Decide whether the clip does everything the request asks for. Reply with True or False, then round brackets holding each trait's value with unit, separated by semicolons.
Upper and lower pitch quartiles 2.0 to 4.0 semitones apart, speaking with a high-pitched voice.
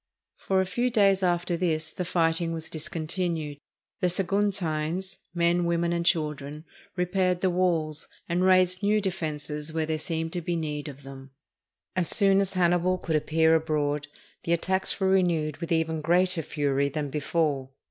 False (2.9 semitones; 170 Hz)